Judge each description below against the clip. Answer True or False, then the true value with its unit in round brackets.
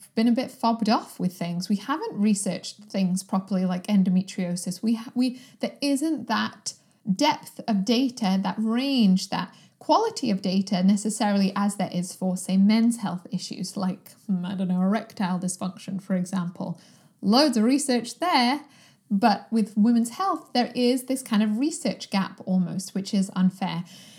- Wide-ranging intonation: False (4.1 semitones)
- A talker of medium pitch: False (205 Hz)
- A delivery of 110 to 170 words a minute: True (160 wpm)